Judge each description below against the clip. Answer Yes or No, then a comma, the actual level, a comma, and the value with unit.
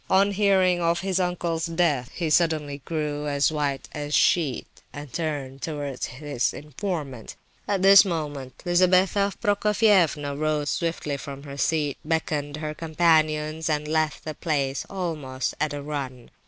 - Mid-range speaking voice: Yes, medium, 155 Hz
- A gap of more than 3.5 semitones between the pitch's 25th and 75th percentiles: No, average, 3.2 semitones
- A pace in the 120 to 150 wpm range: Yes, average, 145 wpm